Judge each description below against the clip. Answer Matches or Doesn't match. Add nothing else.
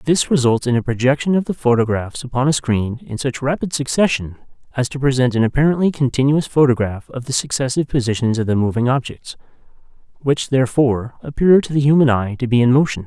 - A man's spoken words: Matches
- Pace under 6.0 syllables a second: Doesn't match